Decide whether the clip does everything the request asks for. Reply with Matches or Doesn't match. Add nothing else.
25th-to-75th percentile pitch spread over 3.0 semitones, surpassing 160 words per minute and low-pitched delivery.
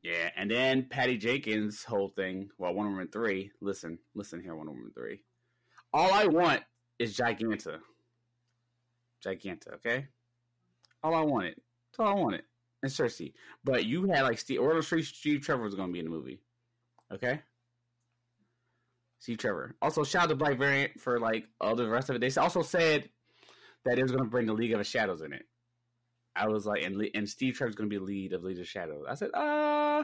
Matches